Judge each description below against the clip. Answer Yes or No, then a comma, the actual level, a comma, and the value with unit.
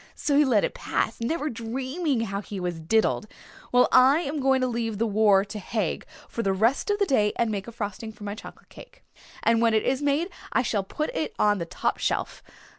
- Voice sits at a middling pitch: No, high, 230 Hz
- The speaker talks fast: Yes, fast, 225 wpm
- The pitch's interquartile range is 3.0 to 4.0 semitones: No, average, 4.4 semitones